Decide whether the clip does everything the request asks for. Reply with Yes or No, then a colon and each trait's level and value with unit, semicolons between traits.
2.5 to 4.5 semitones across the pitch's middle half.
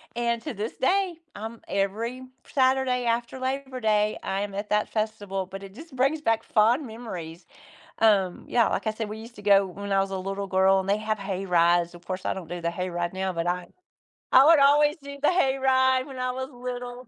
No: average, 5.0 semitones